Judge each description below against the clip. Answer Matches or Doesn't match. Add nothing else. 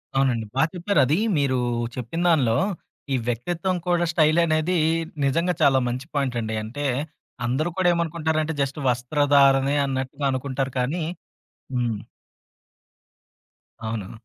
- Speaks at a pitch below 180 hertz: Matches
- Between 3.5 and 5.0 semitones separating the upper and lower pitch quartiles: Matches